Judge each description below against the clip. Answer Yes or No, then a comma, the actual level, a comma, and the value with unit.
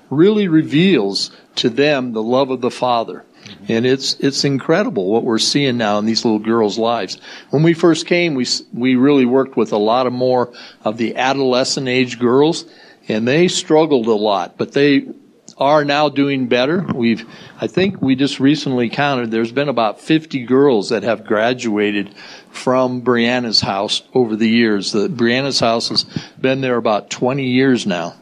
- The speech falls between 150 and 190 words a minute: Yes, average, 175 wpm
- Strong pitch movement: No, average, 3.3 semitones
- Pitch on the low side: Yes, low, 130 Hz